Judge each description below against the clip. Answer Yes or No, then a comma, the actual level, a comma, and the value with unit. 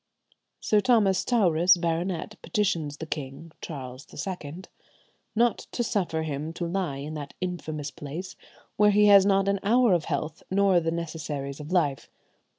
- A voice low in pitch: No, medium, 170 Hz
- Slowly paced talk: No, average, 155 wpm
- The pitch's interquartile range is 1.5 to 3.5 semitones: No, average, 4.6 semitones